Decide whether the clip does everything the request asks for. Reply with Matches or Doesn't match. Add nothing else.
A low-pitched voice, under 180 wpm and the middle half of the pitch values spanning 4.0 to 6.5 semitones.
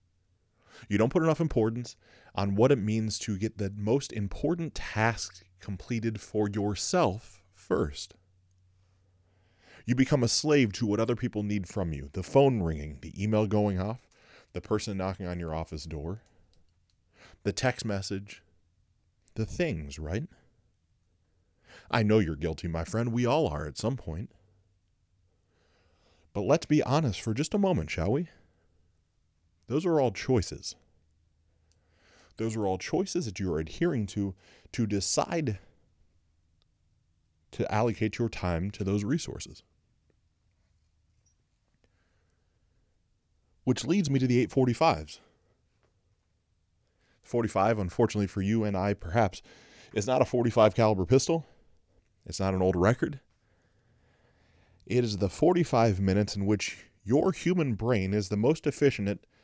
Matches